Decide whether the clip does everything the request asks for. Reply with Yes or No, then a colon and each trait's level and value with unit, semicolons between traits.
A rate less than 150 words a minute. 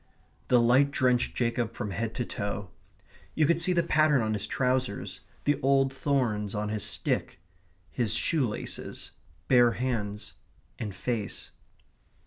Yes: average, 140 wpm